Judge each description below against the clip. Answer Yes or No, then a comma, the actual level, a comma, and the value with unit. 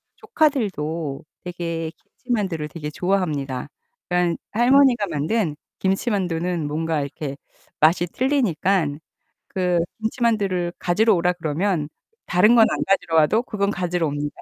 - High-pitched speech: No, medium, 180 Hz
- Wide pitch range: No, average, 4.9 semitones